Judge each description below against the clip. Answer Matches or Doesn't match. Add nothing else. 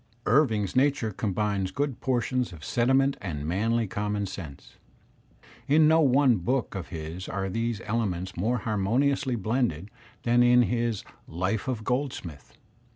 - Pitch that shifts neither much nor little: Matches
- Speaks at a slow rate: Doesn't match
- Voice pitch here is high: Doesn't match